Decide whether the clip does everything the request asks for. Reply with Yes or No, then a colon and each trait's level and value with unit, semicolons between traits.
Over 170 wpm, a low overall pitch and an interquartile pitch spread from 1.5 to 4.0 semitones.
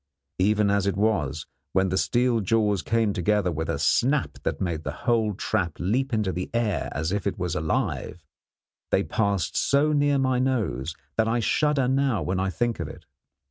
No: average, 185 wpm; low, 105 Hz; average, 4.9 semitones